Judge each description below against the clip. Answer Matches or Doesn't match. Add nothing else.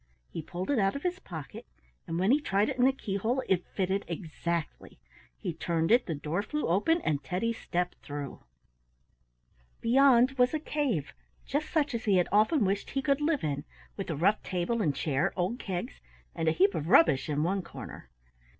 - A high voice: Matches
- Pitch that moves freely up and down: Matches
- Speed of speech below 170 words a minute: Doesn't match